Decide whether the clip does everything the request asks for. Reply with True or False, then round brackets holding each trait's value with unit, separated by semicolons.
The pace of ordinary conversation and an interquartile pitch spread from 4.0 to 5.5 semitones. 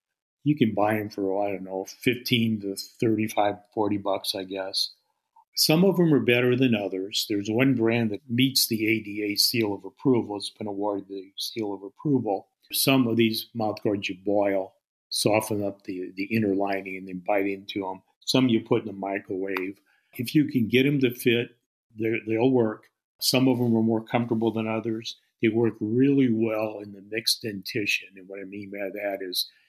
False (190 wpm; 3.4 semitones)